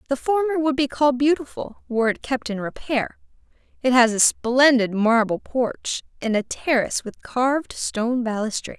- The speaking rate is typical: Yes, average, 165 wpm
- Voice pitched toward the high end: Yes, very high, 250 Hz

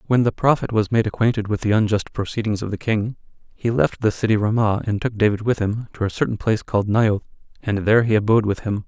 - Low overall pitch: Yes, low, 110 Hz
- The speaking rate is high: Yes, fast, 235 wpm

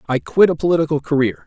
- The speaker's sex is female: No, male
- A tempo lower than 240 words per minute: Yes, fast, 205 wpm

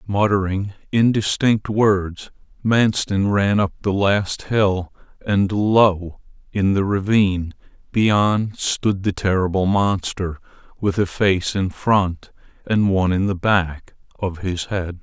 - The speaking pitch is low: Yes, low, 100 Hz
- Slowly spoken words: Yes, slow, 130 wpm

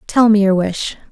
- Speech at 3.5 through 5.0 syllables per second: Yes, 4.7 syllables/s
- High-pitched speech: Yes, high, 205 Hz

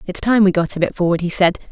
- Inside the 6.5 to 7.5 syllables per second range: Yes, 6.8 syllables/s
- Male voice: No, female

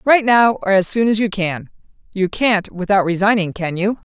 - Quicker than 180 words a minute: Yes, fast, 205 wpm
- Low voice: No, high, 200 Hz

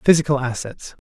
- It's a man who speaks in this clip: Yes, male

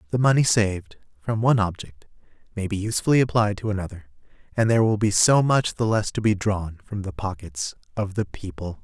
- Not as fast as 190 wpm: No, average, 195 wpm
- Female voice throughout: No, male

